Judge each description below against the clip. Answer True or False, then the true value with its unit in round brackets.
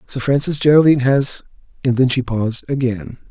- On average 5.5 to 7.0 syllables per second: True (5.7 syllables/s)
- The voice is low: True (130 Hz)